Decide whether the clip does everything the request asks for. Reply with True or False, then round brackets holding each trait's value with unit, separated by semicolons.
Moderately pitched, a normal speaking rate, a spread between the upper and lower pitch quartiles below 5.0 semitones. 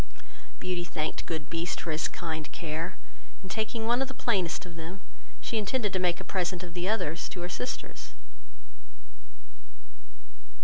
True (175 Hz; 160 wpm; 3.1 semitones)